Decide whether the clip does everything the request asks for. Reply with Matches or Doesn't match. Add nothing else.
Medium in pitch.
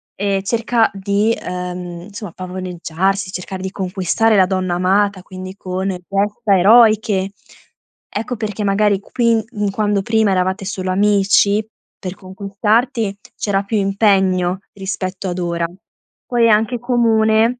Doesn't match